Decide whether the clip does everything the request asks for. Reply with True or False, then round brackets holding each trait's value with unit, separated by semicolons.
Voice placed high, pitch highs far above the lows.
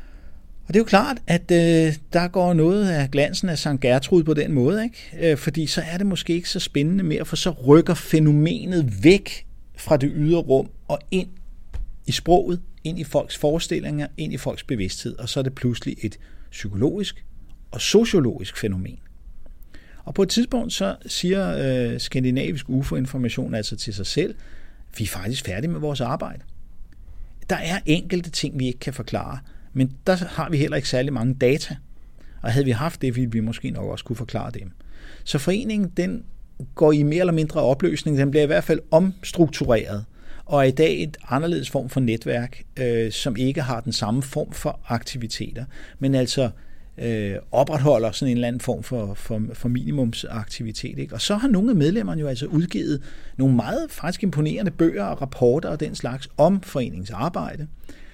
False (140 Hz; 5.9 semitones)